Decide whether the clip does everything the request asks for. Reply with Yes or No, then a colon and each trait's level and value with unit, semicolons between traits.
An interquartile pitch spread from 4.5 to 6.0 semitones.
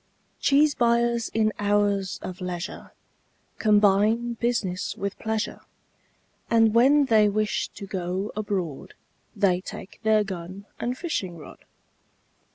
No: average, 3.5 semitones